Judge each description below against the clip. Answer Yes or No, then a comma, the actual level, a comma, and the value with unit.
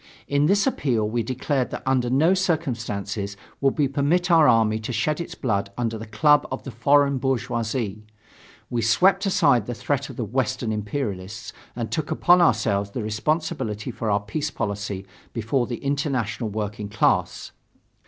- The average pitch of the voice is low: Yes, low, 120 Hz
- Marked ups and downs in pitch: No, average, 4.9 semitones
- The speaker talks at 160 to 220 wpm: Yes, average, 165 wpm